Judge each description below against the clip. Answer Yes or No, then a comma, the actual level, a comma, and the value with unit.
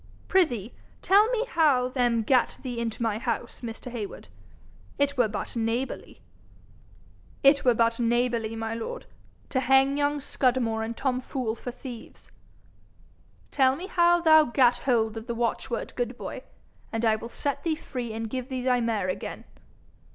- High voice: Yes, high, 245 Hz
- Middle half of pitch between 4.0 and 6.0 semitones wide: No, average, 3.0 semitones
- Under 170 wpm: Yes, average, 160 wpm